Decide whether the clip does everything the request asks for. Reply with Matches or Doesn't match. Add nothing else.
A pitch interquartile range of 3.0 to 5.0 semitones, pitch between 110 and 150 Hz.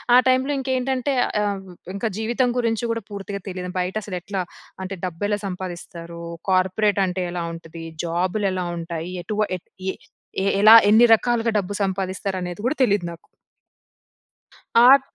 Doesn't match